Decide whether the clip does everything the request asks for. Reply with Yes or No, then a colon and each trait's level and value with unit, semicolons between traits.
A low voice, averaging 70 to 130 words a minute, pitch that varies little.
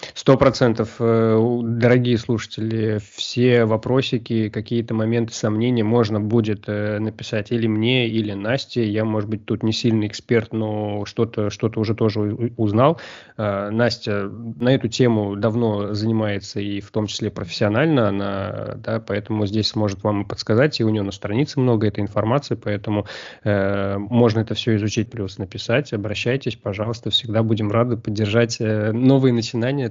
No: low, 110 Hz; average, 140 wpm; narrow, 2.0 semitones